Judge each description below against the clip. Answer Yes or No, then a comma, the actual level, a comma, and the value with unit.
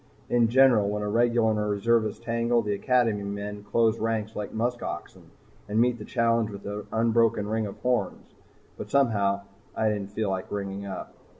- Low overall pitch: Yes, low, 110 Hz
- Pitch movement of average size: No, narrow, 2.2 semitones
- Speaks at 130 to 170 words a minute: No, average, 180 wpm